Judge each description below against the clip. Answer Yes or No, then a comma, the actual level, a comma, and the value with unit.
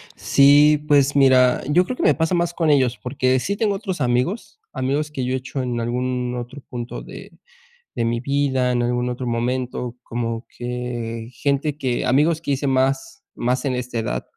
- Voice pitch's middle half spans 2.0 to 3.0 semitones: Yes, average, 2.7 semitones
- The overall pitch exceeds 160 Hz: No, low, 130 Hz